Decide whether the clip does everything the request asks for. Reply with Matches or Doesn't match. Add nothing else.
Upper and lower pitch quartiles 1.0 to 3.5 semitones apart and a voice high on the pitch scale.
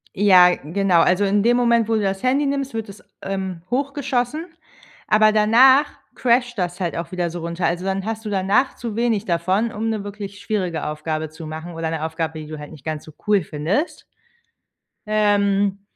Doesn't match